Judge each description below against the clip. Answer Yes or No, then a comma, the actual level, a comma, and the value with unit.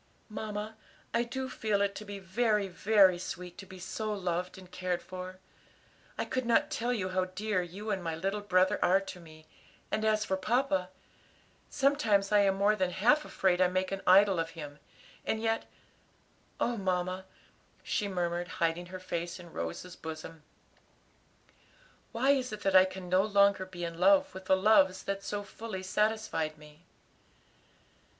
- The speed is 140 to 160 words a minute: No, average, 170 wpm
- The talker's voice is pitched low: No, high, 190 Hz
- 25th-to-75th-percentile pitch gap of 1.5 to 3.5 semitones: Yes, average, 2.8 semitones